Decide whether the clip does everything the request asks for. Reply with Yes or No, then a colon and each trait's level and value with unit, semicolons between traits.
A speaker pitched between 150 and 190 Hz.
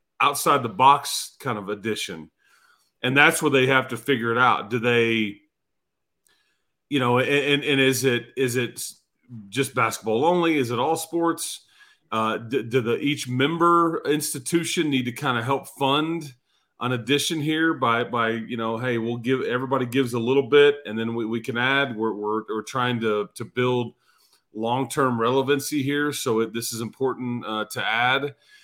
No: low, 130 Hz